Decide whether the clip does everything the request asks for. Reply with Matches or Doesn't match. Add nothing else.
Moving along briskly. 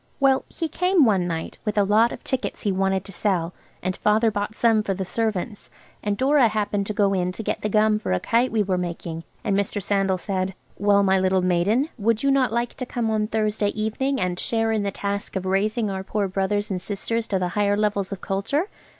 Matches